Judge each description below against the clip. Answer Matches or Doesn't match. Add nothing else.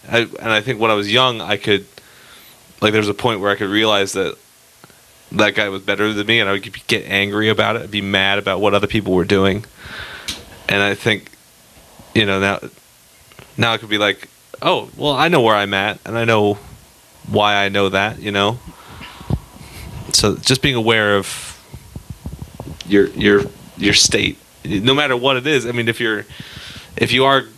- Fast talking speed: Doesn't match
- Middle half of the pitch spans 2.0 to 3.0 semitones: Matches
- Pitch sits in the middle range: Doesn't match